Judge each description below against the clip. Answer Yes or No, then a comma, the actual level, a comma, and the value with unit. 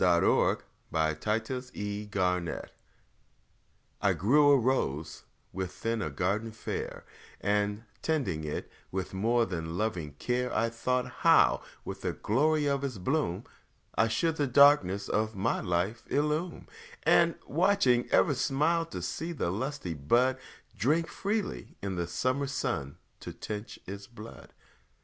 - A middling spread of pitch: No, wide, 7.3 semitones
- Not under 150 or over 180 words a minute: No, slow, 135 wpm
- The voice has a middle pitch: No, low, 115 Hz